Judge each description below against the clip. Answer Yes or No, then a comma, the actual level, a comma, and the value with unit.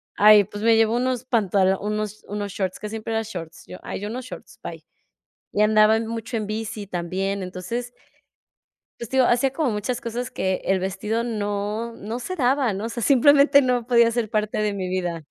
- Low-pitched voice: No, high, 215 Hz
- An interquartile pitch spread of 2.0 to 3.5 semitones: Yes, average, 3.0 semitones